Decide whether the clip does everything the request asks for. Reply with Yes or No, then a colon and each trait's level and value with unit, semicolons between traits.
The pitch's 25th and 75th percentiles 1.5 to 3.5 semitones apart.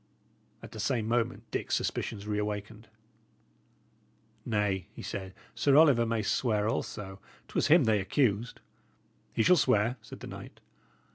Yes: average, 2.9 semitones